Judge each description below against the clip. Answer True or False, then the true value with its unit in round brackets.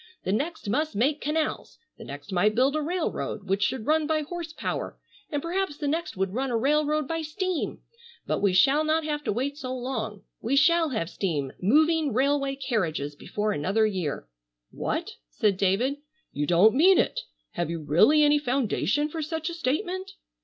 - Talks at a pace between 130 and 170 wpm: False (180 wpm)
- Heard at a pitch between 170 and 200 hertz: False (275 Hz)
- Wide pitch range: True (7.2 semitones)